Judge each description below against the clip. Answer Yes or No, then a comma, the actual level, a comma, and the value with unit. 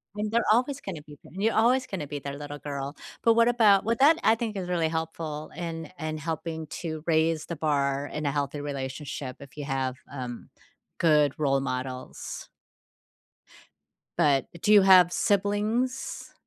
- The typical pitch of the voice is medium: Yes, medium, 160 Hz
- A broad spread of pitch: Yes, wide, 6.1 semitones